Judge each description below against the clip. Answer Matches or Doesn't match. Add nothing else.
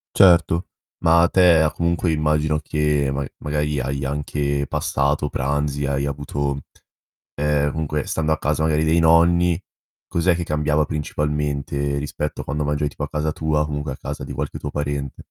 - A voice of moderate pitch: Doesn't match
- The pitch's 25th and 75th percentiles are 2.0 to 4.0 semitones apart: Doesn't match